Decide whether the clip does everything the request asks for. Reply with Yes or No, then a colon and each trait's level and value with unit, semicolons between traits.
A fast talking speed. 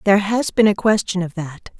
Yes: fast, 235 wpm